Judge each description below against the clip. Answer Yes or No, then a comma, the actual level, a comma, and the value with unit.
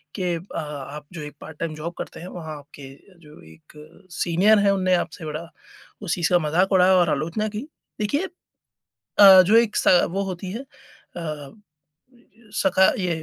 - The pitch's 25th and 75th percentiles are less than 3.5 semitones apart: No, average, 3.9 semitones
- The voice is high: No, medium, 175 Hz